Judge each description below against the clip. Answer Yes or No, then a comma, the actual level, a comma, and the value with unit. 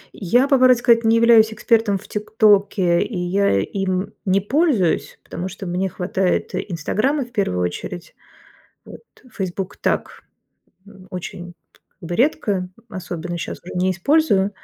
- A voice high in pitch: Yes, high, 195 Hz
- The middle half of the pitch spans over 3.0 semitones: Yes, average, 3.9 semitones